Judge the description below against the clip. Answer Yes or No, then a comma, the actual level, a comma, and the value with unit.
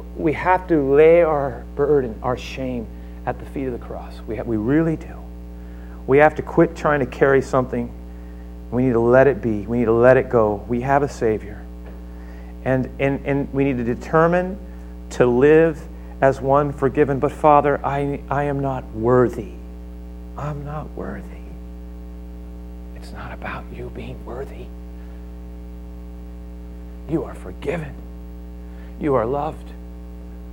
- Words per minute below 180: Yes, average, 150 wpm